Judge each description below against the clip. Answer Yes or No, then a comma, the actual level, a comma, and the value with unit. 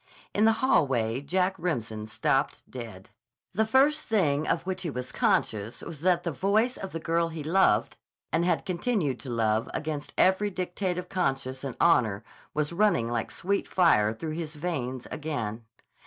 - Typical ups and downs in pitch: No, wide, 6.8 semitones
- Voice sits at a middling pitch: Yes, medium, 160 Hz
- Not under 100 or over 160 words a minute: No, average, 170 wpm